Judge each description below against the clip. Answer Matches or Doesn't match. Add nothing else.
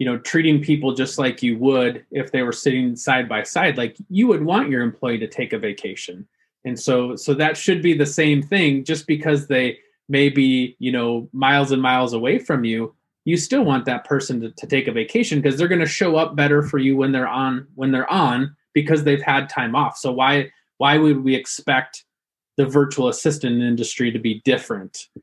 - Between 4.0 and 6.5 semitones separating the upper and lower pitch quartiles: Doesn't match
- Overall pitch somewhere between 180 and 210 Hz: Doesn't match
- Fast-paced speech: Matches